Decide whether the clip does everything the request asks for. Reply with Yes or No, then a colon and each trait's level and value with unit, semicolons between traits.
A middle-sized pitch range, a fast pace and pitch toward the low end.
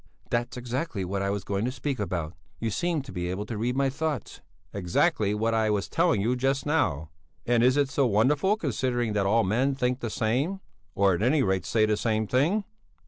Yes: average, 4.7 semitones; fast, 210 wpm; low, 120 Hz